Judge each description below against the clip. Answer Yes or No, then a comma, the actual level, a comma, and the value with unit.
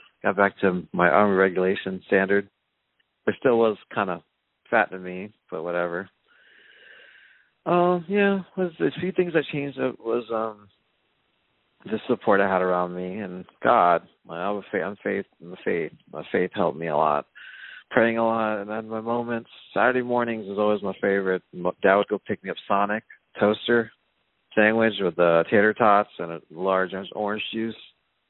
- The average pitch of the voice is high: No, low, 105 Hz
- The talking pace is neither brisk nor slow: Yes, average, 170 wpm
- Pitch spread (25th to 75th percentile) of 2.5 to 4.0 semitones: Yes, average, 3.5 semitones